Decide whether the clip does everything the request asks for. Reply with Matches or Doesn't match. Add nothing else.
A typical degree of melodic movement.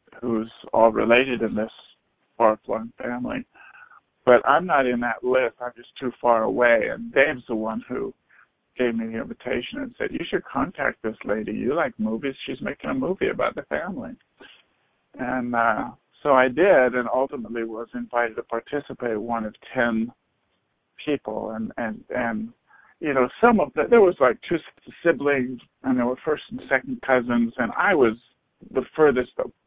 Doesn't match